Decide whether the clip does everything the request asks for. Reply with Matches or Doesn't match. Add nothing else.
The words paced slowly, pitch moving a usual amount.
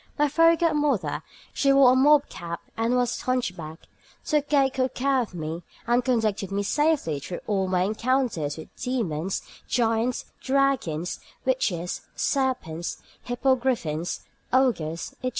Doesn't match